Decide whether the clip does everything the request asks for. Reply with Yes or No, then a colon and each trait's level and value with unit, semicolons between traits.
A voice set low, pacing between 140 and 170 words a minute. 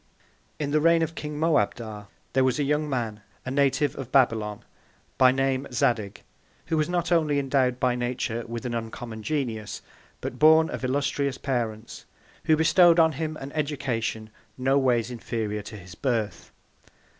Yes: low, 130 Hz; average, 160 wpm